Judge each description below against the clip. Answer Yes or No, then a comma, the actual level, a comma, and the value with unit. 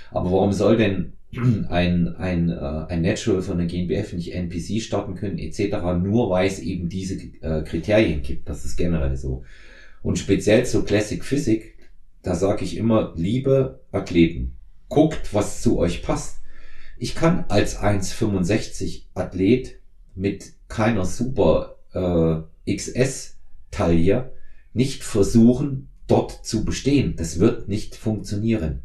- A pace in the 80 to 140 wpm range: Yes, slow, 125 wpm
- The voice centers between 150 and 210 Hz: No, very low, 95 Hz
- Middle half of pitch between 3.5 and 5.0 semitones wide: Yes, average, 4.4 semitones